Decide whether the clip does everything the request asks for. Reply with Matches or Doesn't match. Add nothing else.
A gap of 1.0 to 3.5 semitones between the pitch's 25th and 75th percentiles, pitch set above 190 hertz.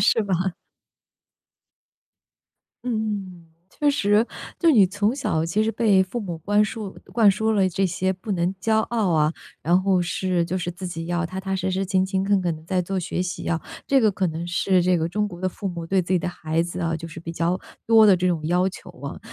Doesn't match